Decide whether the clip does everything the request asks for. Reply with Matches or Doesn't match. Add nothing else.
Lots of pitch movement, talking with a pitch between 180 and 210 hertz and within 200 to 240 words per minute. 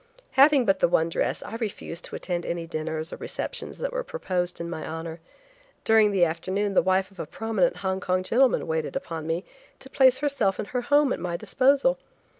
Matches